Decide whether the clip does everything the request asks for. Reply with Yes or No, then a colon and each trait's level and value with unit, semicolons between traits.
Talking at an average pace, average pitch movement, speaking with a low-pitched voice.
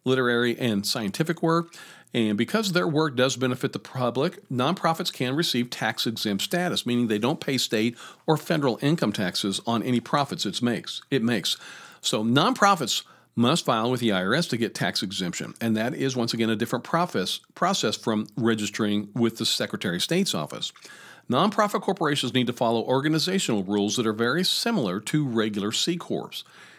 No: average, 170 wpm; wide, 6.7 semitones; low, 130 Hz